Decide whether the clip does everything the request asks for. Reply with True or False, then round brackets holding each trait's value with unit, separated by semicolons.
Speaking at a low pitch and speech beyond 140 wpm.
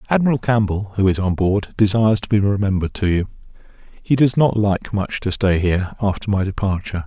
True (100 Hz; 195 wpm)